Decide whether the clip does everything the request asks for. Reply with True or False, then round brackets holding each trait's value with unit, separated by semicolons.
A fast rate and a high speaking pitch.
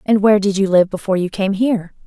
True (260 wpm; 200 Hz)